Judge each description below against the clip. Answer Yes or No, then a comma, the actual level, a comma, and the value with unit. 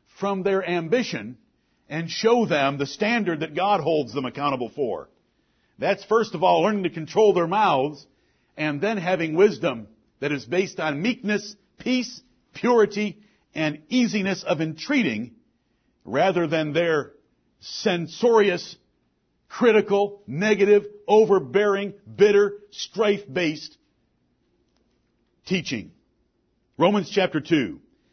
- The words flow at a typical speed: No, slow, 110 wpm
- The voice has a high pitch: Yes, high, 195 Hz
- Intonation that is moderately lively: Yes, average, 4.6 semitones